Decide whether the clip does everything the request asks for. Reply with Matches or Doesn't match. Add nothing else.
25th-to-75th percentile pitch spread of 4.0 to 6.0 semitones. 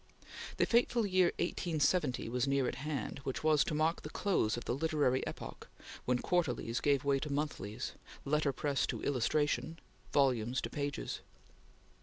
Doesn't match